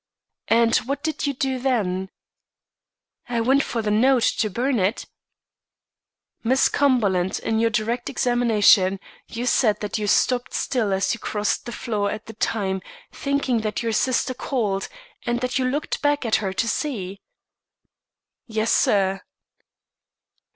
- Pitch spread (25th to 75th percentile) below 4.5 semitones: Yes, average, 3.6 semitones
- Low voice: No, high, 230 Hz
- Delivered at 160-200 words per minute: No, average, 145 wpm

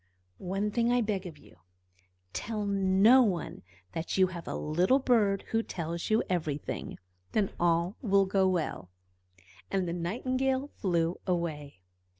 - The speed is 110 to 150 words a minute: Yes, average, 145 wpm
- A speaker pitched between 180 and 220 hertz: Yes, high, 190 Hz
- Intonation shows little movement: No, average, 4.2 semitones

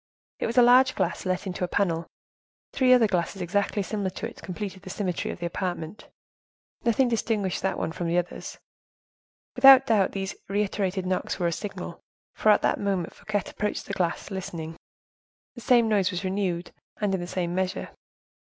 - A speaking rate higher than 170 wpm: Yes, average, 180 wpm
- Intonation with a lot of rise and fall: No, average, 2.8 semitones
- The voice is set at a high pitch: Yes, high, 195 Hz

